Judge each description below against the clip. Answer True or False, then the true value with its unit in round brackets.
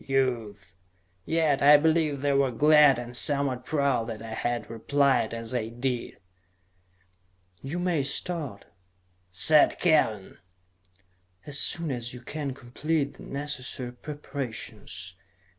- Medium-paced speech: False (120 wpm)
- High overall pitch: False (135 Hz)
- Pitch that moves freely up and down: False (3.8 semitones)